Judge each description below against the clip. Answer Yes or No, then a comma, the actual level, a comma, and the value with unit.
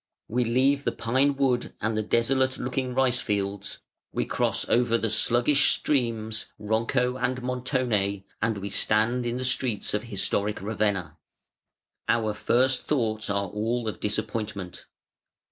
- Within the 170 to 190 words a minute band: No, average, 140 wpm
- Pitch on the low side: Yes, low, 115 Hz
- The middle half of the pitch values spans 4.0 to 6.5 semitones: No, average, 3.2 semitones